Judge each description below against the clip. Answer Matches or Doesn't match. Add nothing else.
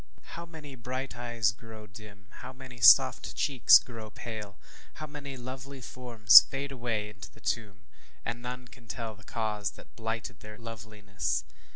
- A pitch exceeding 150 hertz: Doesn't match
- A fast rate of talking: Doesn't match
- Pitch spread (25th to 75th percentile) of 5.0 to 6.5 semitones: Doesn't match